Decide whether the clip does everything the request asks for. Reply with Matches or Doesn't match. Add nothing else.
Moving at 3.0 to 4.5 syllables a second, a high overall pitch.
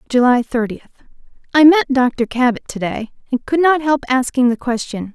Doesn't match